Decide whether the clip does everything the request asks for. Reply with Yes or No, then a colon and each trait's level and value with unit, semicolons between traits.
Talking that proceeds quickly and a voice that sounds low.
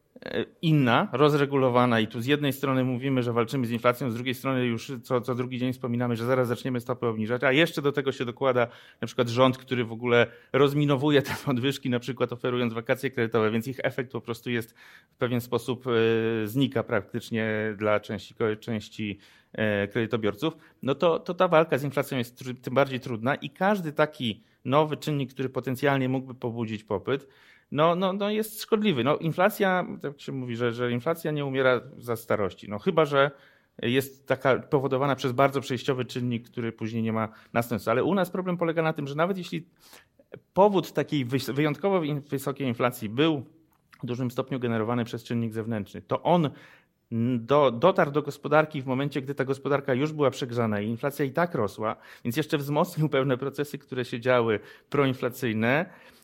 Yes: fast, 180 wpm; low, 130 Hz